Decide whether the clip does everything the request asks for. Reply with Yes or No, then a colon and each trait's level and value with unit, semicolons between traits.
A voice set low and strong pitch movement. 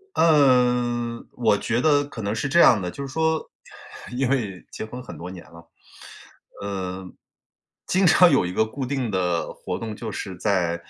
Yes: low, 115 Hz; wide, 6.3 semitones